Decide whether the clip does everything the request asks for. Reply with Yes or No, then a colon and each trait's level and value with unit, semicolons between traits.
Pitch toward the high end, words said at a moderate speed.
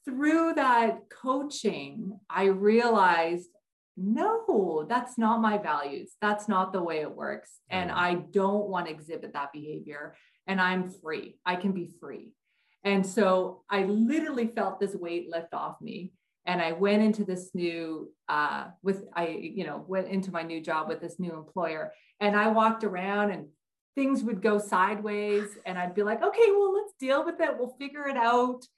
Yes: high, 200 Hz; average, 175 wpm